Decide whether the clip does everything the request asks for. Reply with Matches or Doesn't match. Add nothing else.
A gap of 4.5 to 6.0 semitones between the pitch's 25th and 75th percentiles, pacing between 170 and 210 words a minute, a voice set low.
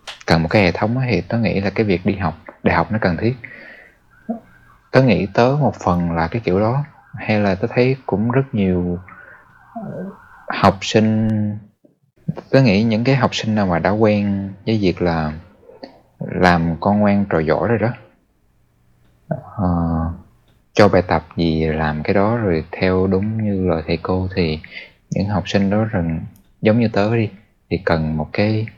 Doesn't match